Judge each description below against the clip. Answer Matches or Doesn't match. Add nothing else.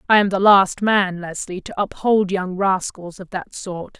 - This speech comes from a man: Doesn't match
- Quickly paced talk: Doesn't match